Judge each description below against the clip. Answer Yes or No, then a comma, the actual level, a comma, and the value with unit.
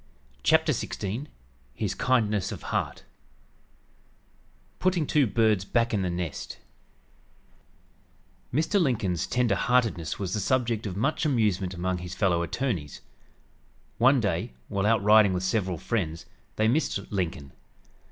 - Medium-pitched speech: No, low, 105 Hz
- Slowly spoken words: Yes, slow, 130 wpm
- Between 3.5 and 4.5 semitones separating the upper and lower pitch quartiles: No, average, 5.0 semitones